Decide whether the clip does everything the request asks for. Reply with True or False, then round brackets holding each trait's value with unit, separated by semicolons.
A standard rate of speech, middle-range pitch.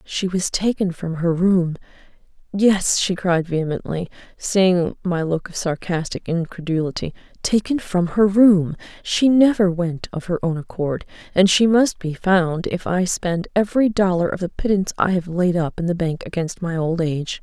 True (175 wpm; 180 Hz)